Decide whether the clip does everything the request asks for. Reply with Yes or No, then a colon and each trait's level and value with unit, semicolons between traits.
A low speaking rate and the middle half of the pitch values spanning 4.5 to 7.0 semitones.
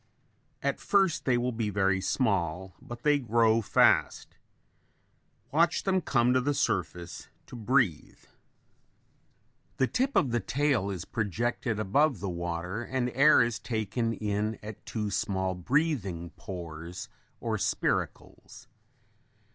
Yes: slow, 125 wpm; average, 5.2 semitones